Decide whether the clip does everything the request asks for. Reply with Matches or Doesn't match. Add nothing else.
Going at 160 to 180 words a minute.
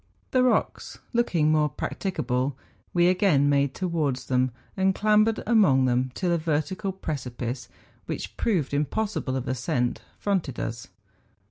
Doesn't match